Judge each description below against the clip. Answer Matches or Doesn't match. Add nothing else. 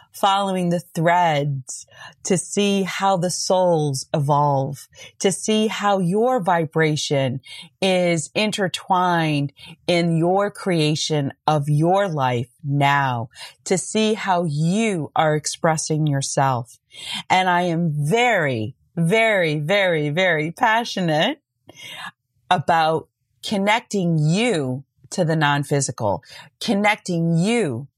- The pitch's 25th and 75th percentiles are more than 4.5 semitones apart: Matches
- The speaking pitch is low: Doesn't match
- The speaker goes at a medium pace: Doesn't match